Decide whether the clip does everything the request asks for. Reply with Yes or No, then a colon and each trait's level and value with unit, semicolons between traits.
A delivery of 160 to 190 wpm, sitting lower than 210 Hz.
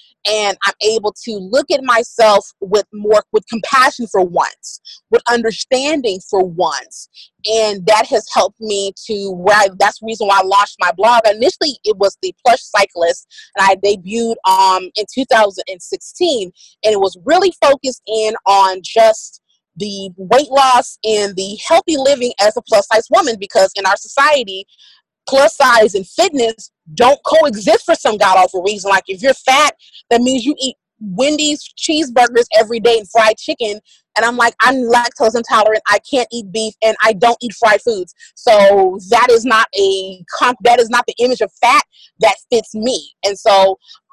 No: average, 175 wpm; high, 220 Hz